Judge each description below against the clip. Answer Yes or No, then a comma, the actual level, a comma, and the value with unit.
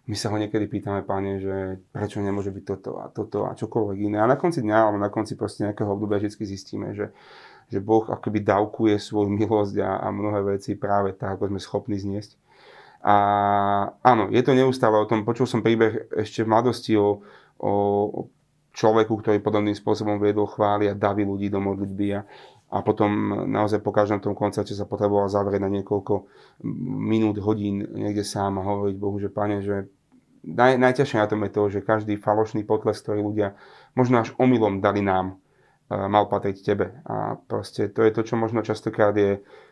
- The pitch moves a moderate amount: No, narrow, 1.2 semitones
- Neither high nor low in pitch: No, low, 105 Hz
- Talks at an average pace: No, fast, 185 wpm